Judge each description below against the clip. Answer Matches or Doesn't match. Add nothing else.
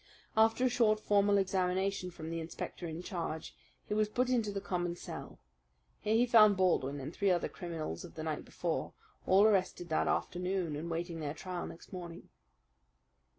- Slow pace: Doesn't match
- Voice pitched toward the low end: Doesn't match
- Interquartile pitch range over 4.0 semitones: Doesn't match